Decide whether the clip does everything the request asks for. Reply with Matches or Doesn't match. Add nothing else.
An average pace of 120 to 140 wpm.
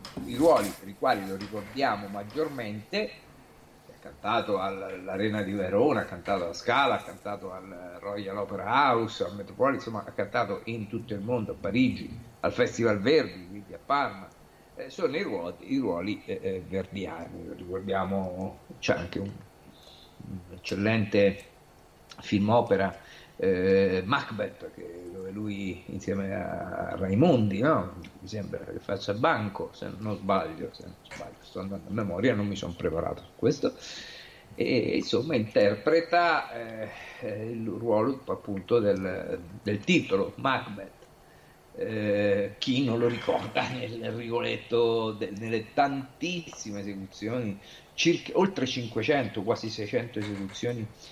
Matches